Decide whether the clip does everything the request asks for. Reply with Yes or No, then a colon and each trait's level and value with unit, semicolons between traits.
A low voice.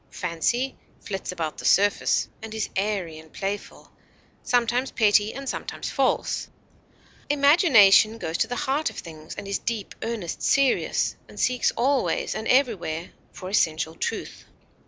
No: high, 215 Hz